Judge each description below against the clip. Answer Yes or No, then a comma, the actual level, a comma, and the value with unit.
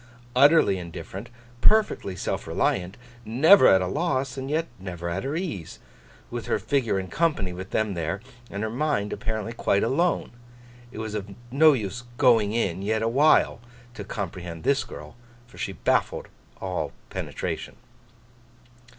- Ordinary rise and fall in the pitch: No, wide, 6.0 semitones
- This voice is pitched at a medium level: No, low, 110 Hz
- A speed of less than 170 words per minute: Yes, average, 145 wpm